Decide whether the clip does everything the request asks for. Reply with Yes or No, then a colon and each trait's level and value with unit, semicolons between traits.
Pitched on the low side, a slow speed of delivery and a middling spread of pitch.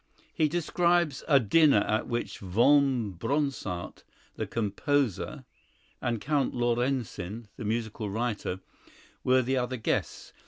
Yes: low, 120 Hz; slow, 115 wpm; average, 4.5 semitones